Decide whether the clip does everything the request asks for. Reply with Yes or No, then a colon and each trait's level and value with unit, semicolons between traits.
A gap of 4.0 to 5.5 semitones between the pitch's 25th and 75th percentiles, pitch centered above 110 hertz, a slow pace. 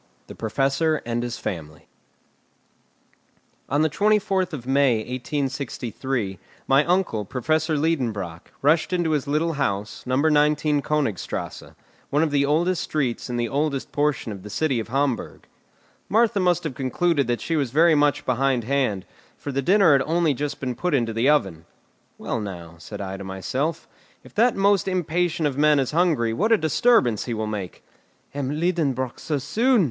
No: average, 5.2 semitones; medium, 140 Hz; average, 165 wpm